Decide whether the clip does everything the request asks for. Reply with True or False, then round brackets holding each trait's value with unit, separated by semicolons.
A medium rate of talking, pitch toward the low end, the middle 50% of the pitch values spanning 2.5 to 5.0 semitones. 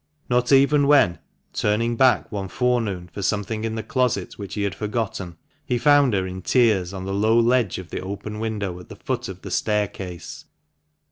True (190 wpm; 105 Hz; 3.8 semitones)